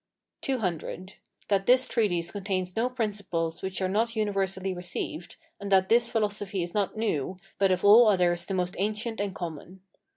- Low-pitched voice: No, high, 195 Hz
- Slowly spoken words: No, average, 165 wpm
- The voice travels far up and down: No, average, 2.9 semitones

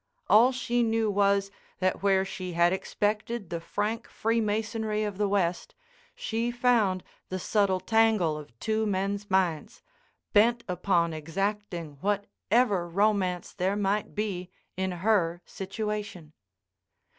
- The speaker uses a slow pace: Yes, slow, 120 wpm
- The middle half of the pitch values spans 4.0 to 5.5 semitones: No, average, 3.0 semitones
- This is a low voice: No, high, 200 Hz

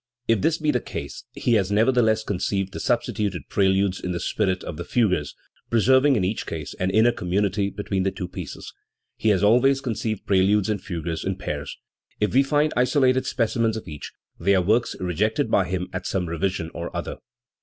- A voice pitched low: Yes, low, 100 Hz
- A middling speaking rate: Yes, average, 185 wpm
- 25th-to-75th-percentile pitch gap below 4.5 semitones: Yes, average, 4.0 semitones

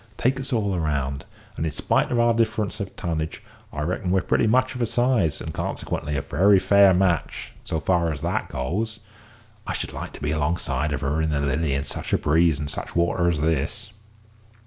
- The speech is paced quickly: Yes, fast, 210 wpm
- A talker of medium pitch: No, very low, 85 Hz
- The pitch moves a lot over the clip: Yes, wide, 6.0 semitones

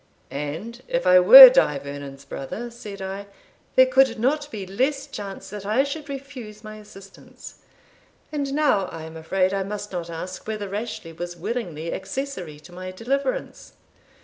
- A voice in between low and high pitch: No, high, 205 Hz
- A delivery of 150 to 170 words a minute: Yes, average, 160 wpm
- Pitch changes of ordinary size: No, wide, 6.3 semitones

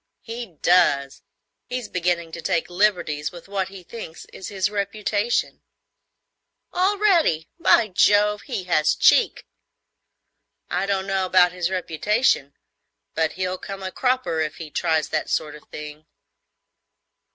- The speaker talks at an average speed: No, slow, 130 wpm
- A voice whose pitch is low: No, medium, 185 Hz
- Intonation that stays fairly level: No, average, 4.1 semitones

